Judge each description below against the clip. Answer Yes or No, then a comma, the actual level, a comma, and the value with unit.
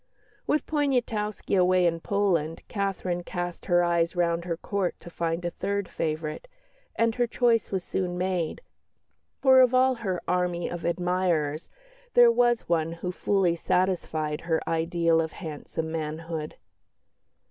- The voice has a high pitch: No, medium, 175 Hz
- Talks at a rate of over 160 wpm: No, average, 140 wpm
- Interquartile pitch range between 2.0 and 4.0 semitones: Yes, average, 3.3 semitones